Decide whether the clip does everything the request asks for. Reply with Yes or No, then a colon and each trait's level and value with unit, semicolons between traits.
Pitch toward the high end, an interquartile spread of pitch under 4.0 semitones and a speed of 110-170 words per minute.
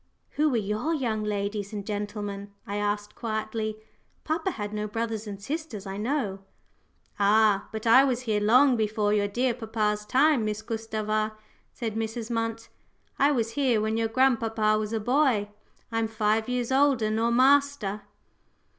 Yes: high, 220 Hz; narrow, 2.6 semitones; average, 155 wpm